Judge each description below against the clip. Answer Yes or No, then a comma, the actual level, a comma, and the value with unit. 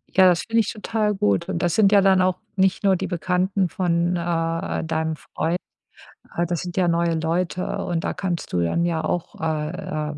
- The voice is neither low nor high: Yes, medium, 175 Hz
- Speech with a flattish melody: Yes, narrow, 2.3 semitones